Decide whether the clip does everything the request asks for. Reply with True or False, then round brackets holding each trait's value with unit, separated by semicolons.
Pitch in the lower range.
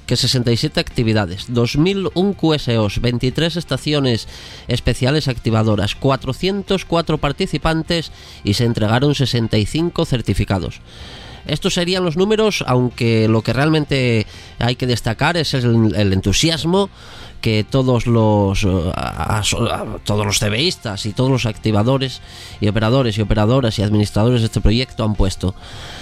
True (120 Hz)